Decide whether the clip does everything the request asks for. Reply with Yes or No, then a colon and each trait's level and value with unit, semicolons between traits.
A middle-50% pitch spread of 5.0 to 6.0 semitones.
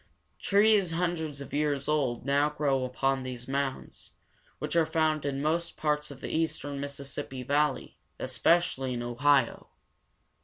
No: narrow, 2.6 semitones